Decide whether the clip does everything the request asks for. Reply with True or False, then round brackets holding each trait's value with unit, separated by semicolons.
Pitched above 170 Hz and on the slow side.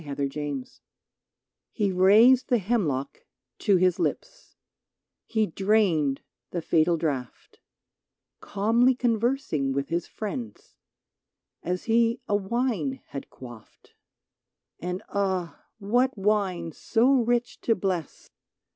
True (190 Hz; 110 wpm)